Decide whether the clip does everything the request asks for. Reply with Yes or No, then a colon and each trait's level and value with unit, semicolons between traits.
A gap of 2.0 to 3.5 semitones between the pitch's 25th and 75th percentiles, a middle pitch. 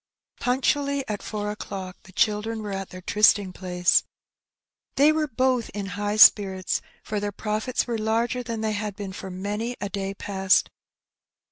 No: average, 2.8 semitones; high, 210 Hz